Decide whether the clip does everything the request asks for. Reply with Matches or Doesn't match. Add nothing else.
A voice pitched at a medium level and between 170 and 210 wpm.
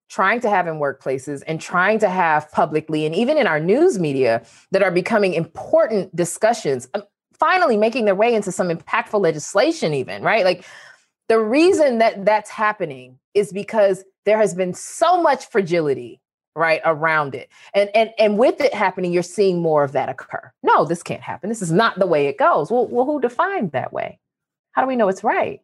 Doesn't match